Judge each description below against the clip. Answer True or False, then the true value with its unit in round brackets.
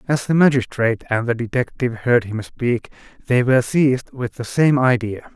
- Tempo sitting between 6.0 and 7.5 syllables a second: False (5.3 syllables/s)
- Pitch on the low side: True (125 Hz)